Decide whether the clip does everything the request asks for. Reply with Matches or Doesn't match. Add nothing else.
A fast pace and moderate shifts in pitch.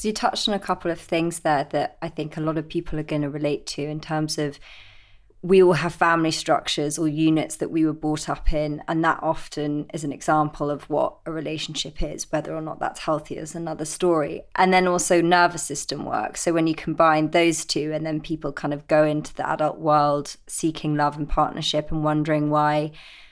Doesn't match